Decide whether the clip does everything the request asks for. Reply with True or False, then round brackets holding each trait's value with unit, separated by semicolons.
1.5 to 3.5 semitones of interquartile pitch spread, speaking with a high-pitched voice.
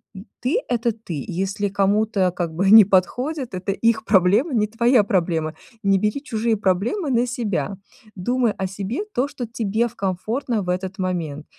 False (4.0 semitones; 205 Hz)